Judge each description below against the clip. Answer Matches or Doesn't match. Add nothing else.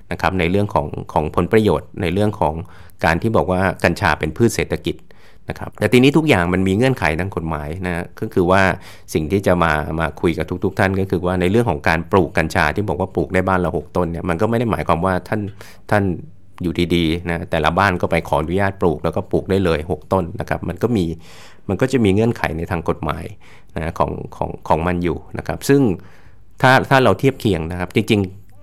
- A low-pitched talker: Matches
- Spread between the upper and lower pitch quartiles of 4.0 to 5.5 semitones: Doesn't match